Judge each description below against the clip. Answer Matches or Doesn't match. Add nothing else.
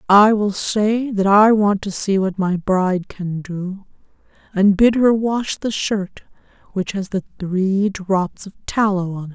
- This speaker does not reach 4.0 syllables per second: Matches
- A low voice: Doesn't match